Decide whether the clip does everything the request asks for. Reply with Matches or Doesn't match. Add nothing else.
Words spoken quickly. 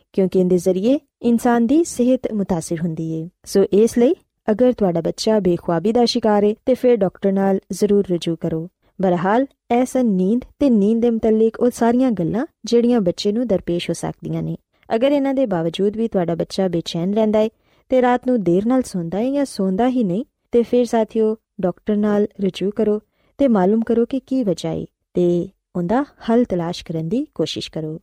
Matches